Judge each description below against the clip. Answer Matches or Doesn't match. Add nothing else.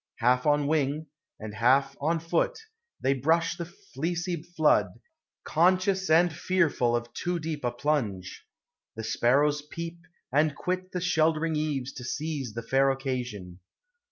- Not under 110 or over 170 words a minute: Matches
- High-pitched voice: Doesn't match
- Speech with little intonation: Doesn't match